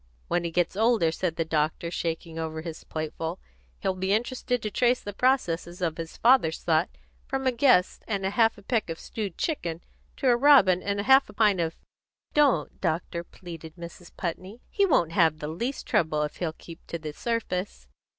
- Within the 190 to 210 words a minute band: Yes, average, 200 wpm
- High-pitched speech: No, medium, 180 Hz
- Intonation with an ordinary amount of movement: No, wide, 5.8 semitones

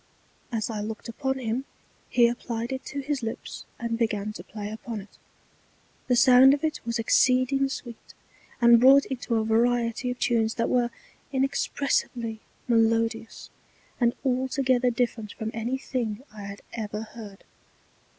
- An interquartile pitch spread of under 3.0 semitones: Yes, narrow, 2.4 semitones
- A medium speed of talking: Yes, average, 150 wpm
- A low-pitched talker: No, high, 235 Hz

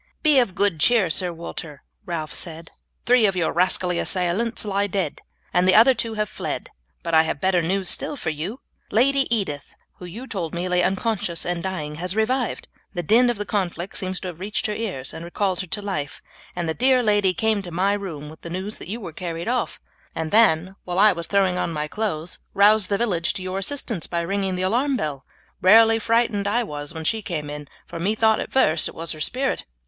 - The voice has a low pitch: No, high, 190 Hz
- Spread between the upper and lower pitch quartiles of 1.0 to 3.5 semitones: No, average, 4.4 semitones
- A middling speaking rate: No, fast, 220 wpm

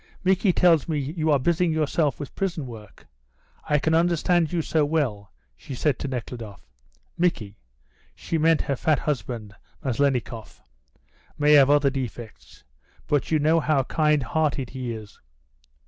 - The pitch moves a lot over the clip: No, average, 4.2 semitones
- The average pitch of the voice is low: No, medium, 145 Hz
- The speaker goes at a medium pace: Yes, average, 145 wpm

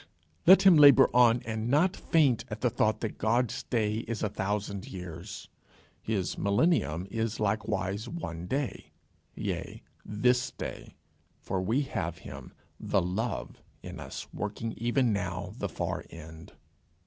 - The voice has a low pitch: Yes, low, 110 Hz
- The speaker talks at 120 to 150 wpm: Yes, average, 140 wpm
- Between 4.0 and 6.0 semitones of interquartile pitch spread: Yes, average, 4.5 semitones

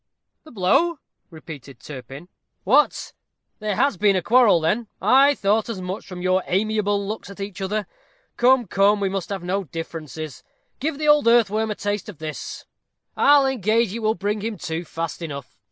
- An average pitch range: Yes, average, 4.2 semitones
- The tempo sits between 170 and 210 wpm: Yes, average, 175 wpm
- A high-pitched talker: Yes, high, 200 Hz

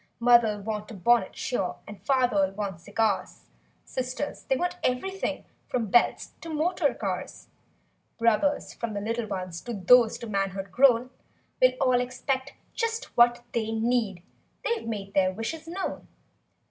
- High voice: Yes, high, 235 Hz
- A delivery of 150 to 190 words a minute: No, slow, 135 wpm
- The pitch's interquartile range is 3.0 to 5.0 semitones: Yes, average, 4.2 semitones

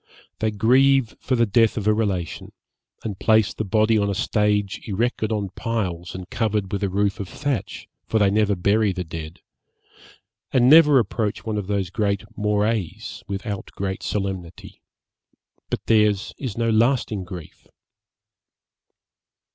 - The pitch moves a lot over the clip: No, narrow, 2.6 semitones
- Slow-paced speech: No, average, 145 wpm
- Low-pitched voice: Yes, low, 105 Hz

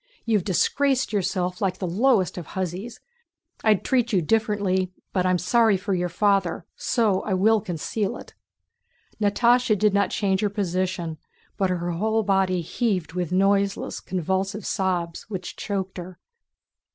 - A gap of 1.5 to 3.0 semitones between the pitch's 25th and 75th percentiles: Yes, average, 2.7 semitones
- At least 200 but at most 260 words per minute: No, average, 145 wpm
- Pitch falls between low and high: No, high, 195 Hz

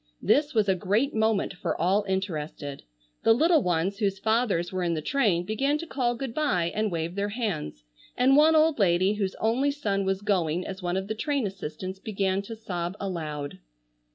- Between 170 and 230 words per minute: Yes, average, 190 wpm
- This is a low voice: No, high, 200 Hz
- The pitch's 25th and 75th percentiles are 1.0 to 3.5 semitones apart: No, average, 4.5 semitones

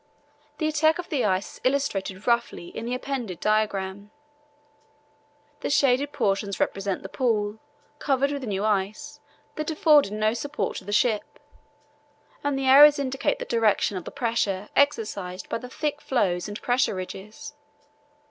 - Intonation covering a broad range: Yes, wide, 5.7 semitones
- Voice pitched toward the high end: Yes, high, 230 Hz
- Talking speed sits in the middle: Yes, average, 150 wpm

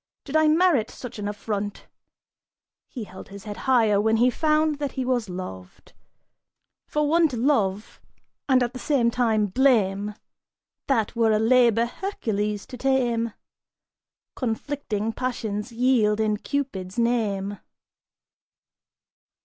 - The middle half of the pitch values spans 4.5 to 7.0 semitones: No, average, 4.0 semitones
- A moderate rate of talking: No, slow, 125 wpm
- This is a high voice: Yes, high, 230 Hz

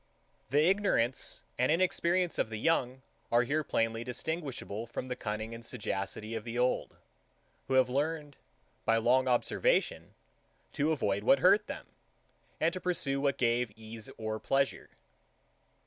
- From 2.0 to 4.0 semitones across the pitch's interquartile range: No, wide, 5.4 semitones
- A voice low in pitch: Yes, low, 125 Hz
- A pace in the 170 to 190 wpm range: No, average, 145 wpm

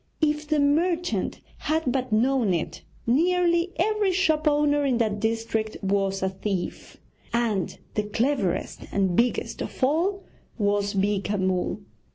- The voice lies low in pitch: No, high, 245 Hz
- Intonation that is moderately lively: No, wide, 7.3 semitones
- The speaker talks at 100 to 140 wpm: Yes, slow, 135 wpm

